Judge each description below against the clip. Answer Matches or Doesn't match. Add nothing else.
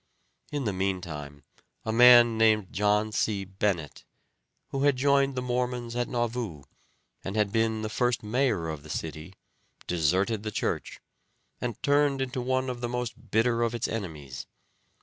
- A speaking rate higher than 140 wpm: Matches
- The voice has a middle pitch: Doesn't match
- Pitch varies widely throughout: Doesn't match